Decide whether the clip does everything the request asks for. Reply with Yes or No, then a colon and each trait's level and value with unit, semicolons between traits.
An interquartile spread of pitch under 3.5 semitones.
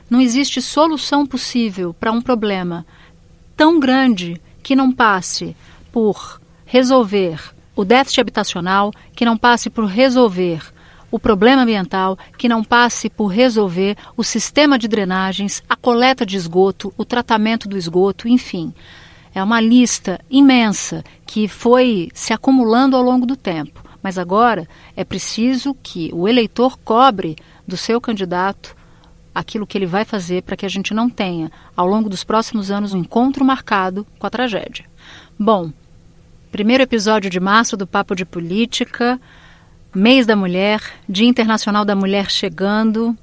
No: average, 4.1 semitones